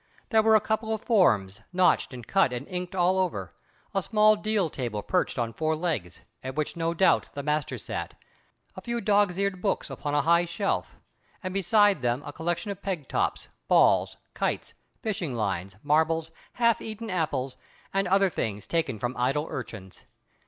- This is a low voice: No, medium, 170 Hz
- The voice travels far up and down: Yes, wide, 7.0 semitones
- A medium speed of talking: Yes, average, 175 wpm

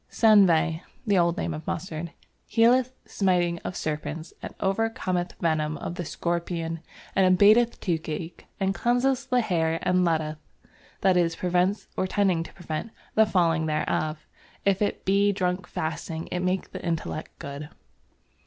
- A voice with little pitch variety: No, average, 3.3 semitones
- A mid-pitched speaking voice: Yes, medium, 175 Hz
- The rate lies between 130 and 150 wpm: Yes, average, 145 wpm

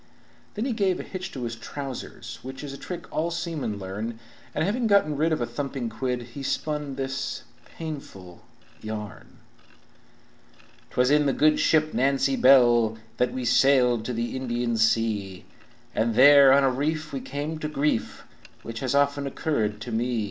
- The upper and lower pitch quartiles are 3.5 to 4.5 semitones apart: Yes, average, 4.2 semitones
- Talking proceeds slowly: No, average, 170 wpm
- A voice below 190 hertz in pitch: Yes, low, 135 Hz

